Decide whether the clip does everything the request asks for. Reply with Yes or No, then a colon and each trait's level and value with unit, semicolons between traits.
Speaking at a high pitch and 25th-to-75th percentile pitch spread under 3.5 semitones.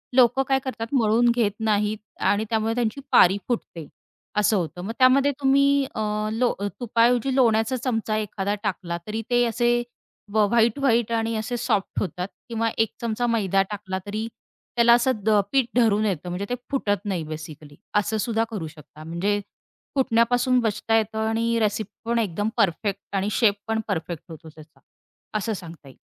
Yes: high, 220 Hz; average, 2.9 semitones